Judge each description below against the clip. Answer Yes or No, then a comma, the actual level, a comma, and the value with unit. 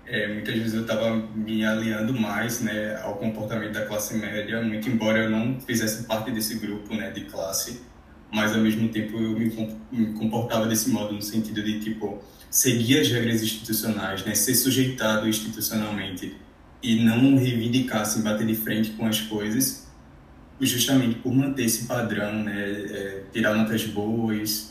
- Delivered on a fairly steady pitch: Yes, narrow, 1.1 semitones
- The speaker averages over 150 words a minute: Yes, average, 160 wpm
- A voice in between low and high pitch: No, low, 110 Hz